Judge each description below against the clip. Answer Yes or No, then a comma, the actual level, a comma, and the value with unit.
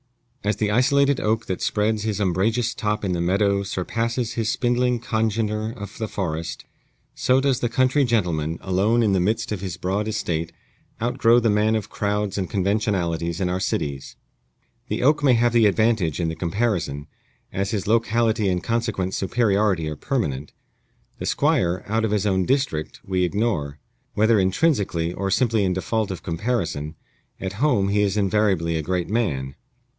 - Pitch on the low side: Yes, low, 105 Hz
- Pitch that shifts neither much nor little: Yes, average, 3.9 semitones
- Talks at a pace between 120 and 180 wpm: Yes, average, 170 wpm